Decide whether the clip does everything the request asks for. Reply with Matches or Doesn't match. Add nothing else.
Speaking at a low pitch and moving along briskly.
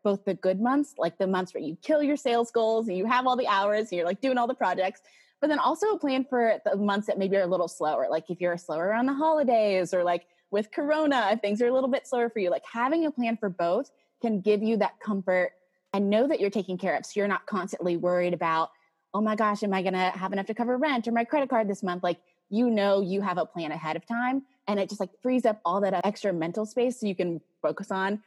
Doesn't match